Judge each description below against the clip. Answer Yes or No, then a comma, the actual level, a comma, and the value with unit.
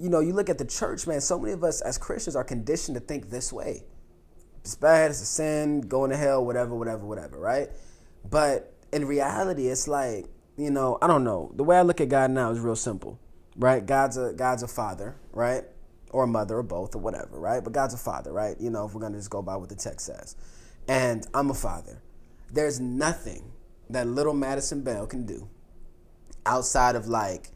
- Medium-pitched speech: No, low, 125 Hz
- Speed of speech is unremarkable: No, fast, 215 wpm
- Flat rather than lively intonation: No, average, 3.9 semitones